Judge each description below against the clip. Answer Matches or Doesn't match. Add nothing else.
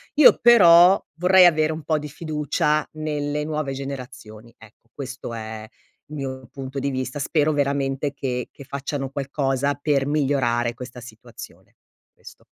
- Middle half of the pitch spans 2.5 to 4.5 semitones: Matches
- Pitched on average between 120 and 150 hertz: Matches